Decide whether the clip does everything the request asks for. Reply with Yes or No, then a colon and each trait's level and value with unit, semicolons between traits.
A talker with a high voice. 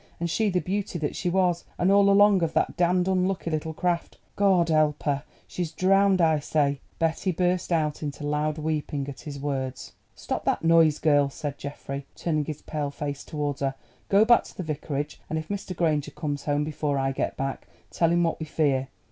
No: medium, 155 Hz